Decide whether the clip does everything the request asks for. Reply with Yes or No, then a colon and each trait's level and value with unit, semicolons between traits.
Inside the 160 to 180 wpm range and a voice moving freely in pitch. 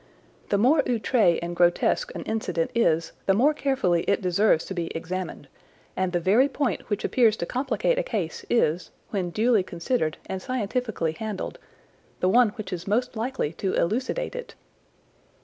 Yes: average, 165 wpm; wide, 6.0 semitones